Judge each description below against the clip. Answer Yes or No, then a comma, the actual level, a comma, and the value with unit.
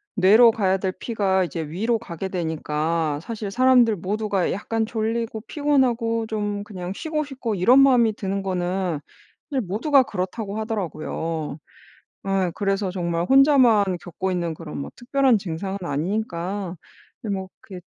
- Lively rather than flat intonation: No, average, 4.2 semitones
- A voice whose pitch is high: Yes, high, 200 Hz